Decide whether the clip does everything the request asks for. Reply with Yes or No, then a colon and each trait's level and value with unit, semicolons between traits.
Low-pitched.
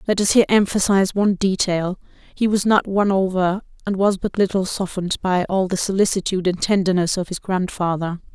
No: high, 190 Hz